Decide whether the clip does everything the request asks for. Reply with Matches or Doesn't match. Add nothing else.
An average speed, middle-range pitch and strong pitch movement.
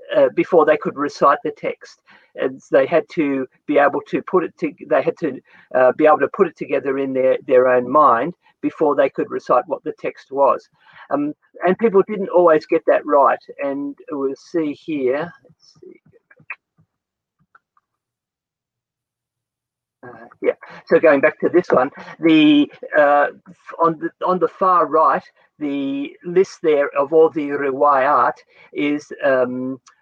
Matches